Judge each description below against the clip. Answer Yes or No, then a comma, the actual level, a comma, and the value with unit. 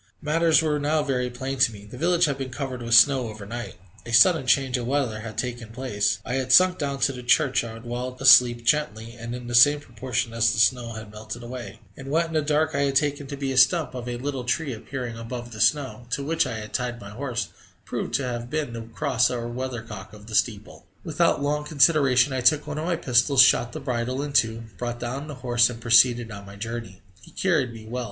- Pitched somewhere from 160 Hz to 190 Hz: No, low, 125 Hz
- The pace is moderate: No, fast, 235 wpm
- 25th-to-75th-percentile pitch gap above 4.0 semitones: No, average, 3.2 semitones